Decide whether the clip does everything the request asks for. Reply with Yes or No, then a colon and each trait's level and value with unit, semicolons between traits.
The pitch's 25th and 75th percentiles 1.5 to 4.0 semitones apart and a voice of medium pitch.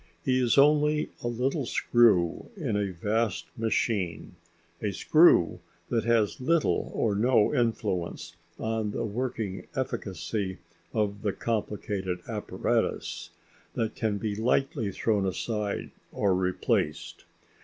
No: average, 3.3 semitones; low, 110 Hz